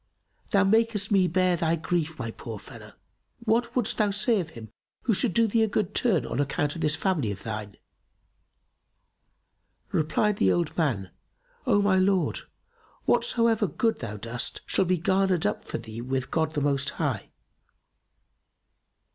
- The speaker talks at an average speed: Yes, average, 160 wpm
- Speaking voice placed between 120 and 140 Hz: No, medium, 170 Hz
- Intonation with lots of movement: Yes, wide, 7.7 semitones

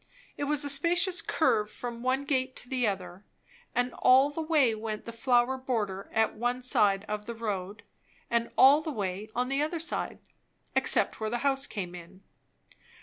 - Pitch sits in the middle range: No, high, 240 Hz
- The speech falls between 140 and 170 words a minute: No, average, 180 wpm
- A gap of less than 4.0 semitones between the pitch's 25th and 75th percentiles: No, average, 4.4 semitones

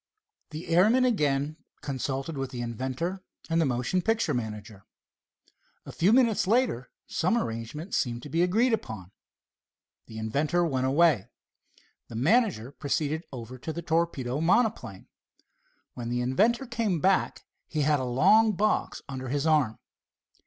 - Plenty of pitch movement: Yes, wide, 6.9 semitones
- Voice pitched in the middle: Yes, medium, 150 Hz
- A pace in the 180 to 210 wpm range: No, average, 140 wpm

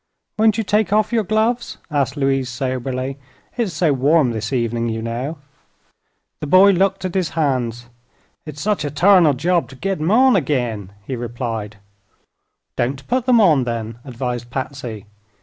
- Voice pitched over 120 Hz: Yes, medium, 140 Hz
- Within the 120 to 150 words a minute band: No, average, 160 wpm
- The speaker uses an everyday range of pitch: No, wide, 7.7 semitones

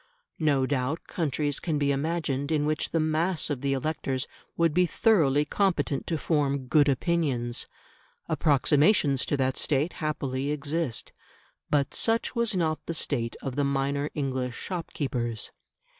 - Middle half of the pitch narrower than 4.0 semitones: Yes, average, 2.9 semitones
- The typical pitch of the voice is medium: Yes, medium, 145 Hz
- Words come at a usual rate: Yes, average, 145 wpm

